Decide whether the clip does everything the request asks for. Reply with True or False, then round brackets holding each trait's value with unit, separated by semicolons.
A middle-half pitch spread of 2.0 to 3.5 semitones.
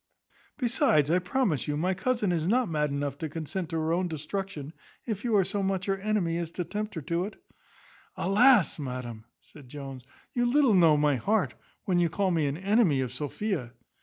False (5.4 semitones)